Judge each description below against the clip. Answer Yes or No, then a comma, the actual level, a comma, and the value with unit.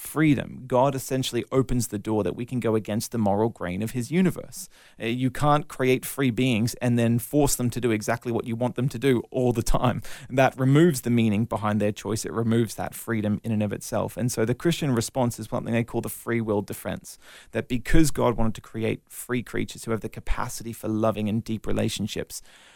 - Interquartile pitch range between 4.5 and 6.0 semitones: No, narrow, 2.5 semitones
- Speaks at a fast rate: Yes, fast, 220 wpm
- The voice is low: Yes, low, 115 Hz